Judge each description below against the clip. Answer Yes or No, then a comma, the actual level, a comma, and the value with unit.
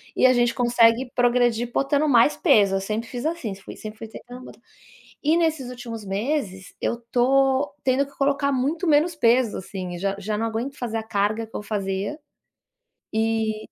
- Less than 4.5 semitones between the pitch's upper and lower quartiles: Yes, average, 4.1 semitones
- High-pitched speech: Yes, high, 240 Hz